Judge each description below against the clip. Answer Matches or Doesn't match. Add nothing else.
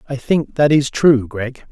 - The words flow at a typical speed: Doesn't match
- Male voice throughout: Matches